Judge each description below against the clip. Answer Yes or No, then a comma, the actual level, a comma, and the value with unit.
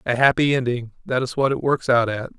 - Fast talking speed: Yes, fast, 250 wpm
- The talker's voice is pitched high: No, low, 125 Hz